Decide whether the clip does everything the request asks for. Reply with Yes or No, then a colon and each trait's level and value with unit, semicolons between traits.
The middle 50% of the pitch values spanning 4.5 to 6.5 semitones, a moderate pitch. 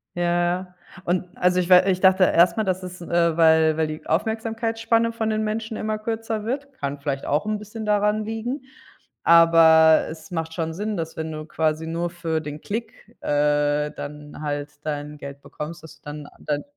Yes: wide, 5.4 semitones; medium, 170 Hz